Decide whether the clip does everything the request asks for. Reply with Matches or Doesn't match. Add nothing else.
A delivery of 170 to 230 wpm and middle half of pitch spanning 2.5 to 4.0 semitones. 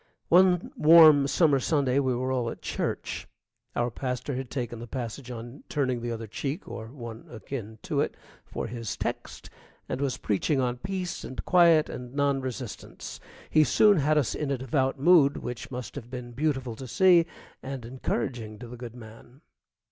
Matches